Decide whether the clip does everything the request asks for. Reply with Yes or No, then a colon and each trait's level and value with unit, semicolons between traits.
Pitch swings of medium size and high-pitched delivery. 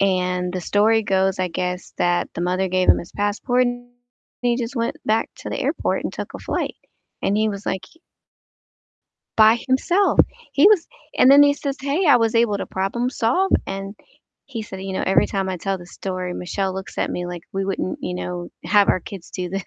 Yes: average, 4.4 semitones; high, 195 Hz